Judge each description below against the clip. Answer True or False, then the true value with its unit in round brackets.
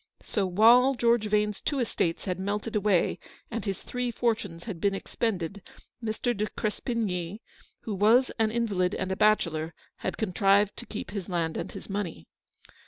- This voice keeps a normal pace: True (165 wpm)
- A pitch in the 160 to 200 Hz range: False (210 Hz)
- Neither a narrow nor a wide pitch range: True (3.4 semitones)